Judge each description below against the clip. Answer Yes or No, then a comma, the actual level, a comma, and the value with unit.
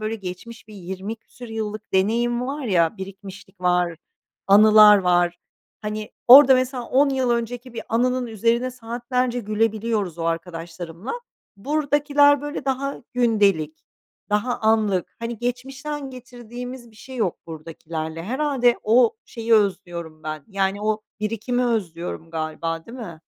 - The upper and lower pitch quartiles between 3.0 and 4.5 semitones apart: No, average, 5.0 semitones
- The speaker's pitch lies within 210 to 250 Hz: Yes, high, 220 Hz